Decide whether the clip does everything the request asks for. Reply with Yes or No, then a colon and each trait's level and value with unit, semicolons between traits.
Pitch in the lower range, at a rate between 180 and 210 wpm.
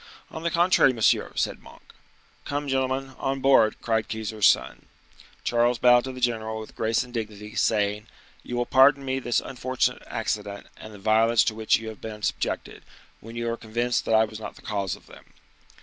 Yes: low, 115 Hz; average, 190 wpm